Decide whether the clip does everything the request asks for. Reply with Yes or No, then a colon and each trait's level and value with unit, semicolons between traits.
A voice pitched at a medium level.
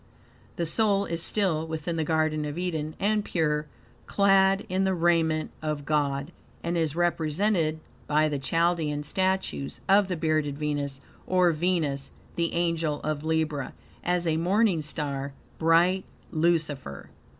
Yes: medium, 160 Hz